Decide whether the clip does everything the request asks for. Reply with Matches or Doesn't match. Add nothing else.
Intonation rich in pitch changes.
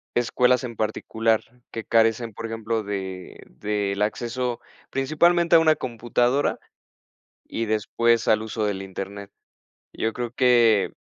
Doesn't match